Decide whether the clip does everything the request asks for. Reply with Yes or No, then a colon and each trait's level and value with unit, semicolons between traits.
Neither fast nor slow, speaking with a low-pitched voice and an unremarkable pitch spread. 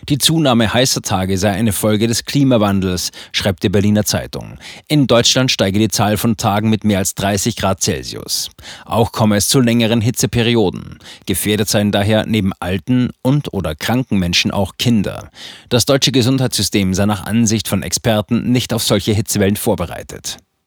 Yes: average, 165 wpm; low, 110 Hz; average, 3.0 semitones